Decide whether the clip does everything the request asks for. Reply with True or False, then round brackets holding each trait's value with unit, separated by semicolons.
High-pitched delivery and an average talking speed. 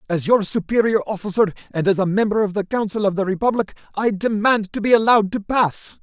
False (205 Hz; 210 wpm)